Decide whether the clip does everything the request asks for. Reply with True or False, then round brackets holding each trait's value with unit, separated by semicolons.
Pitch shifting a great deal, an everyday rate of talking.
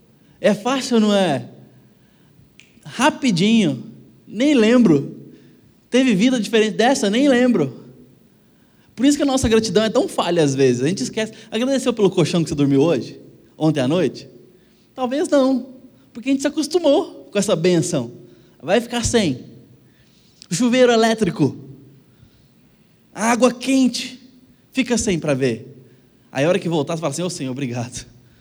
True (9.0 semitones; 150 wpm)